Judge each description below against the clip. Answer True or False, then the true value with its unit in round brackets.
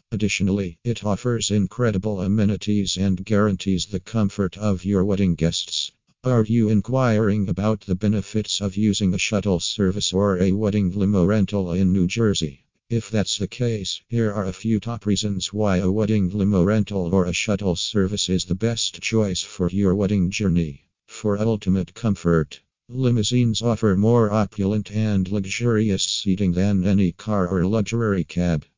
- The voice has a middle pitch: False (100 Hz)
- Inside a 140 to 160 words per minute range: True (155 wpm)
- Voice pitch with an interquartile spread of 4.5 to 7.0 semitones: False (2.4 semitones)